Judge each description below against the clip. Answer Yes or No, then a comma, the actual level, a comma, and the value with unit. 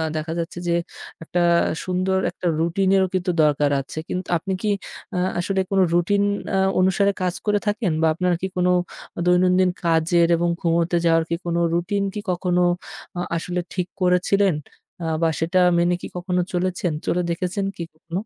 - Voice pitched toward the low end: No, medium, 180 Hz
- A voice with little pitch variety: Yes, narrow, 1.7 semitones